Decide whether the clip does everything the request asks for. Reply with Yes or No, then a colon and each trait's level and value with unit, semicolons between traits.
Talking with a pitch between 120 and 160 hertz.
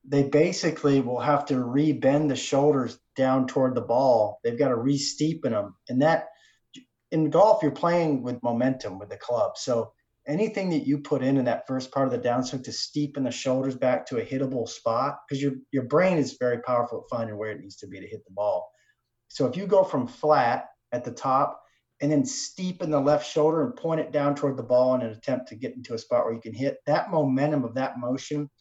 Yes: medium, 140 Hz